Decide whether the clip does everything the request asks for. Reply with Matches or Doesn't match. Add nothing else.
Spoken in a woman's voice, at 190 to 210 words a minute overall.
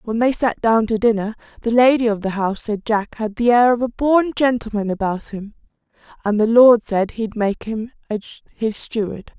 Matches